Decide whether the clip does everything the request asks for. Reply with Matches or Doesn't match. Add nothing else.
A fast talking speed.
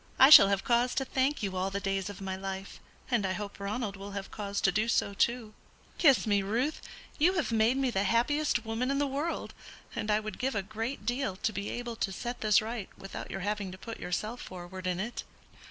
Matches